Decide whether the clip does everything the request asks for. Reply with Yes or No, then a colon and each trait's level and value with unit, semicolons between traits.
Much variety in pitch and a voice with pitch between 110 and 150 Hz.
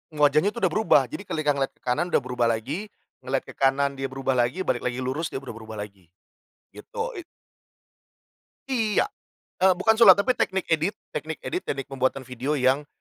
Yes: wide, 6.6 semitones; medium, 140 Hz